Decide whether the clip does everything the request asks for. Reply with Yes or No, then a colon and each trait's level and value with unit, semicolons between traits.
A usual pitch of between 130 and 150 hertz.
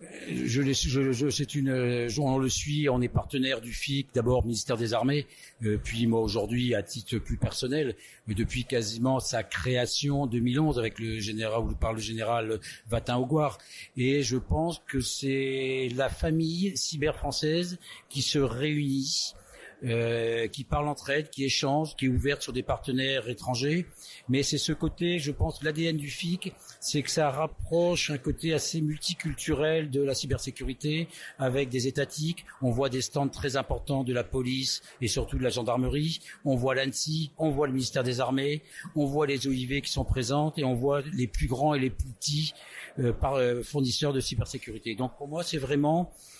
Yes: low, 135 Hz